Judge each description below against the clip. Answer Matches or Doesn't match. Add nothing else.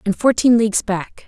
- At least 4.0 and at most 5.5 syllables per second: Matches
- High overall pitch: Matches